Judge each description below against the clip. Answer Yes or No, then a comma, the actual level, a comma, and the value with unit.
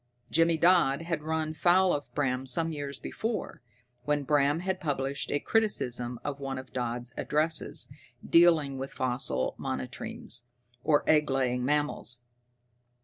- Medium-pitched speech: Yes, medium, 145 Hz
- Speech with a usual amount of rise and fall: Yes, average, 3.8 semitones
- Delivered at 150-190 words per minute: No, slow, 135 wpm